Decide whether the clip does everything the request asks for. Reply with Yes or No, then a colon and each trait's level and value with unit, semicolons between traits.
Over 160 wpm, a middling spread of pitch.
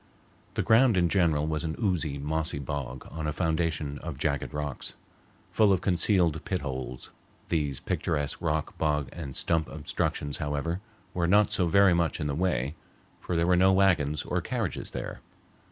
Yes: average, 170 wpm; average, 3.5 semitones